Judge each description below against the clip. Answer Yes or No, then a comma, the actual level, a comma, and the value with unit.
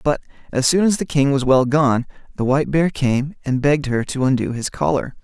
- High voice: No, low, 135 Hz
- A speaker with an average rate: No, fast, 230 wpm